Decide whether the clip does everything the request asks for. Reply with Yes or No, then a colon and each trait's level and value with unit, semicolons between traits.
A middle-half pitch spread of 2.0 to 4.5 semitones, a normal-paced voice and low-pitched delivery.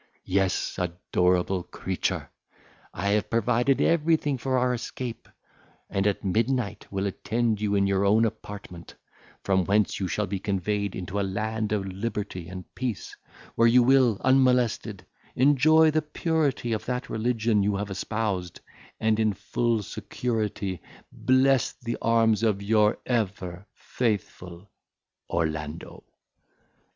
No: average, 3.7 semitones; slow, 130 wpm; low, 105 Hz